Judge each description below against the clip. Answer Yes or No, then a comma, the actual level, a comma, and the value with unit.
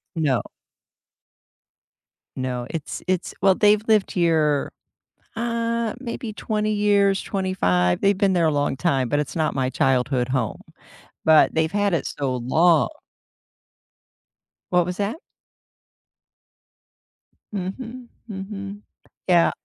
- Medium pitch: Yes, medium, 180 Hz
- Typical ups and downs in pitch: No, wide, 6.1 semitones